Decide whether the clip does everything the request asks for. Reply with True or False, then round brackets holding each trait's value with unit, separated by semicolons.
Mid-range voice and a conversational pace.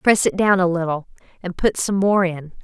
False (180 Hz; 225 wpm)